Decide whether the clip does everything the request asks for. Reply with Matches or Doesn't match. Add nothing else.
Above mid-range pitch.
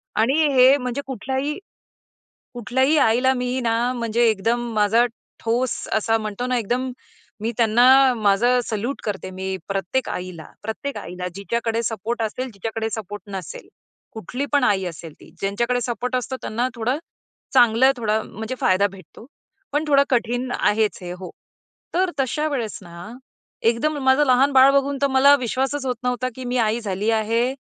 Matches